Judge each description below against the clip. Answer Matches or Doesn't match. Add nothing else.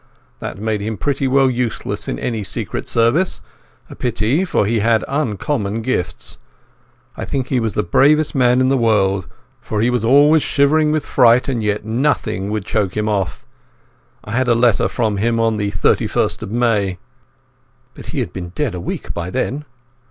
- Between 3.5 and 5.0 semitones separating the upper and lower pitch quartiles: Matches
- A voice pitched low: Matches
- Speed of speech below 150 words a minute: Doesn't match